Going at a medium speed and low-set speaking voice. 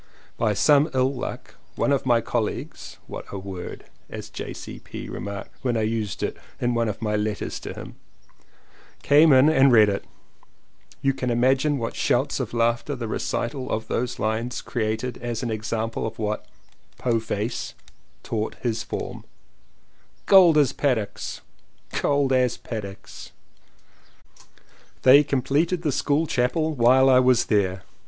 Yes: average, 145 wpm; low, 120 Hz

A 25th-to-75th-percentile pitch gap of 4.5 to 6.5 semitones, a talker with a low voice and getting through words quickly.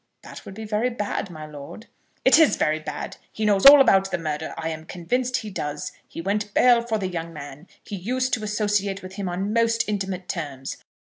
No: average, 5.1 semitones; high, 195 Hz; fast, 210 wpm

